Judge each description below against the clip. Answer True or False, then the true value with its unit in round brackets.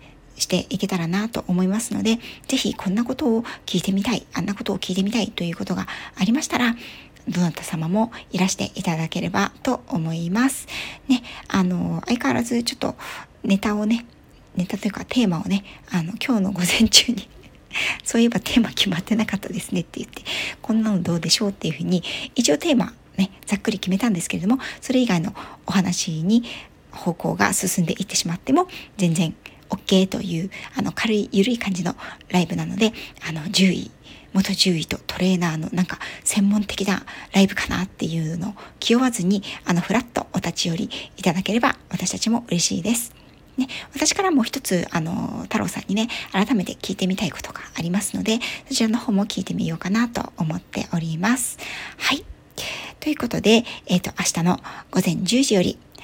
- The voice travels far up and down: False (4.1 semitones)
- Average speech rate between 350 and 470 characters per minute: True (380 characters per minute)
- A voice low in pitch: False (200 Hz)